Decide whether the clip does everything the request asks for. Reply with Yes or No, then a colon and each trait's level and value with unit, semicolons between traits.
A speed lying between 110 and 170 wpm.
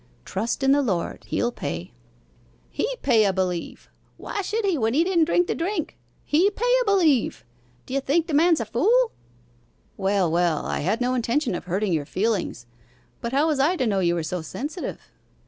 No: average, 190 wpm